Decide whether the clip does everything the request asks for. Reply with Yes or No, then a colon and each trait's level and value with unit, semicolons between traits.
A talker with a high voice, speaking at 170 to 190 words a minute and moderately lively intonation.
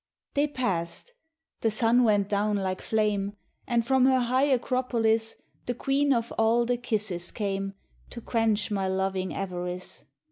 No: high, 220 Hz; average, 145 wpm; average, 3.8 semitones